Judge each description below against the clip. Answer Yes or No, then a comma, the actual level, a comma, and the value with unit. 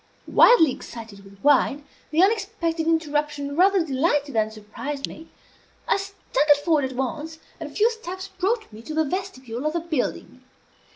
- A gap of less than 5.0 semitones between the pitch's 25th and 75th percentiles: No, wide, 5.4 semitones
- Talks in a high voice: Yes, very high, 305 Hz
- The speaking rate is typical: Yes, average, 160 wpm